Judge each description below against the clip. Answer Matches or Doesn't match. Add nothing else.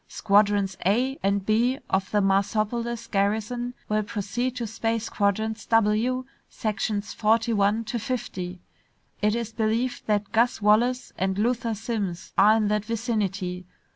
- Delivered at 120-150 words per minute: Matches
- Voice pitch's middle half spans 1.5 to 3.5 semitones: Matches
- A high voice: Matches